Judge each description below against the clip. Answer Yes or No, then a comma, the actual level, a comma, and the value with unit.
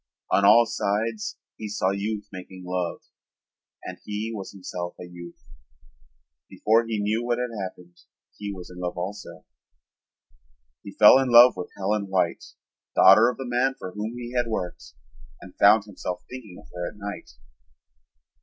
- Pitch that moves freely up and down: No, average, 3.7 semitones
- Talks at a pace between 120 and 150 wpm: No, average, 160 wpm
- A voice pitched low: Yes, low, 105 Hz